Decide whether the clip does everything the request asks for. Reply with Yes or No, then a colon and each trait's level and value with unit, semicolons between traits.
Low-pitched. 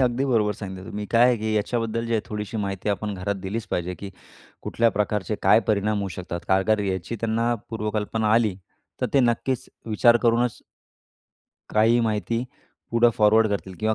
Yes: low, 110 Hz